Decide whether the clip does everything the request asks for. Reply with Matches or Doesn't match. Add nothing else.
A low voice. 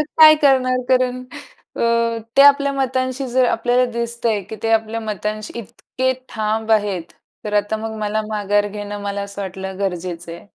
Doesn't match